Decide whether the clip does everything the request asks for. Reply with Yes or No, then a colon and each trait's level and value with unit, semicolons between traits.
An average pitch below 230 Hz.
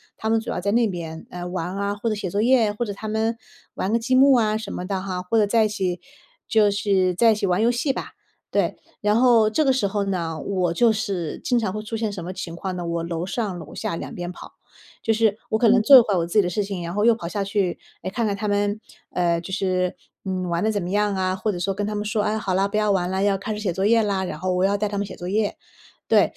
Yes: high, 200 Hz